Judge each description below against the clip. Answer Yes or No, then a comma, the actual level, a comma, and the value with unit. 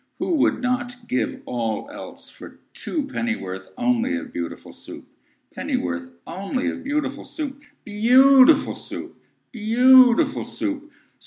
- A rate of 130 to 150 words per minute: Yes, average, 140 wpm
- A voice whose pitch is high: Yes, high, 245 Hz